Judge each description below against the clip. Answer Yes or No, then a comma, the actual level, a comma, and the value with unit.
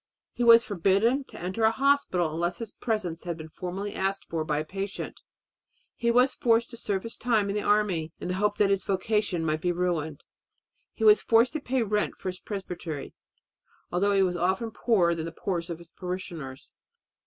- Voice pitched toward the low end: No, high, 195 Hz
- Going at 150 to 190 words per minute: No, average, 200 wpm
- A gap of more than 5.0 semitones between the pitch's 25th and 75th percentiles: No, average, 4.3 semitones